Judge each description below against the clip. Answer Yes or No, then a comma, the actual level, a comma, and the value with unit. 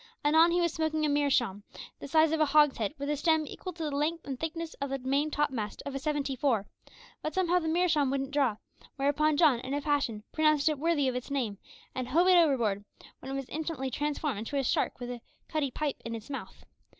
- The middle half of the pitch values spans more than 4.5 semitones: No, average, 3.0 semitones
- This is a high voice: Yes, very high, 290 Hz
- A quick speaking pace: Yes, fast, 225 wpm